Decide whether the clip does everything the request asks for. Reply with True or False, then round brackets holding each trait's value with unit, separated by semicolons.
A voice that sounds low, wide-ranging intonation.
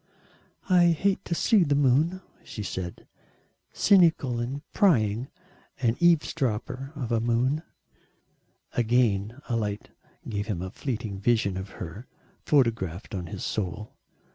True (120 Hz; 5.7 semitones)